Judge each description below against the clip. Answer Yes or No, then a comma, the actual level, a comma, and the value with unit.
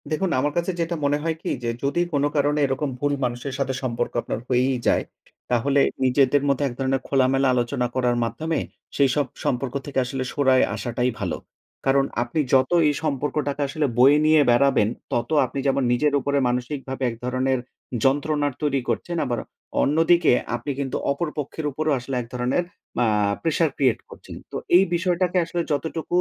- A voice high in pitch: No, medium, 140 Hz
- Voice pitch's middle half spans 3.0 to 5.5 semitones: No, narrow, 2.6 semitones